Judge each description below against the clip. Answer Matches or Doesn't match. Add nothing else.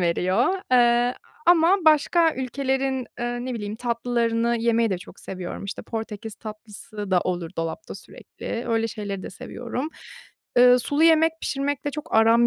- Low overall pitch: Doesn't match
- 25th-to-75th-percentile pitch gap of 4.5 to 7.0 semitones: Doesn't match